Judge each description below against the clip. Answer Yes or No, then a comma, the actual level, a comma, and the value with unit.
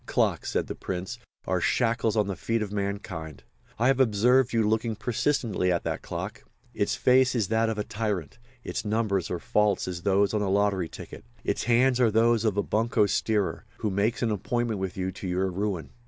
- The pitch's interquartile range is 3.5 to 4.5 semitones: No, average, 3.0 semitones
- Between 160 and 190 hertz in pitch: No, low, 105 Hz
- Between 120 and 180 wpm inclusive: No, average, 200 wpm